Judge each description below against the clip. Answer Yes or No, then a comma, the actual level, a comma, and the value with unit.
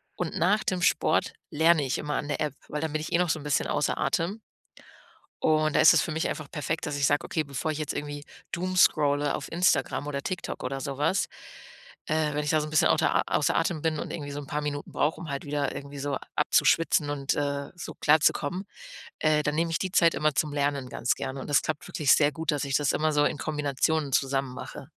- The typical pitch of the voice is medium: Yes, medium, 150 Hz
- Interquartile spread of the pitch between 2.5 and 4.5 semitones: No, narrow, 1.8 semitones